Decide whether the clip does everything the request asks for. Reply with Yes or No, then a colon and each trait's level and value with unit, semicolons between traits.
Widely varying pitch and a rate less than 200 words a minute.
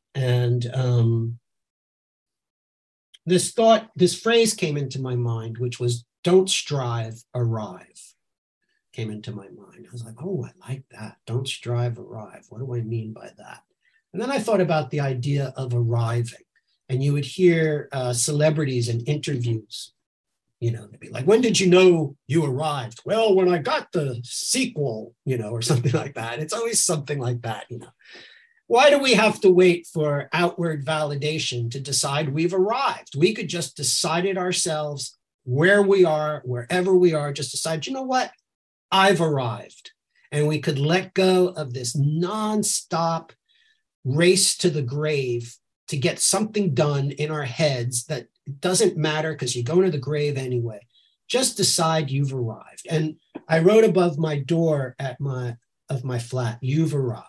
Yes: wide, 6.4 semitones; average, 170 wpm